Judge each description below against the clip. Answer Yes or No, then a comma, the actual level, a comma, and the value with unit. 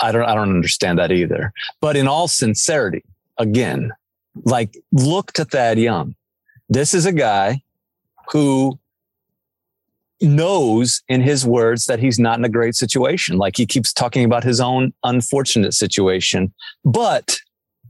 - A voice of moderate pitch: No, low, 120 Hz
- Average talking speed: Yes, average, 145 wpm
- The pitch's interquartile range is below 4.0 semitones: Yes, average, 3.3 semitones